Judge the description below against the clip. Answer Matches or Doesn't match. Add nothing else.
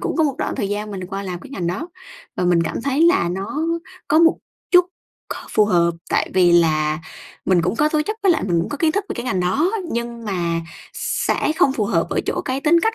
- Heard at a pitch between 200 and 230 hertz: Matches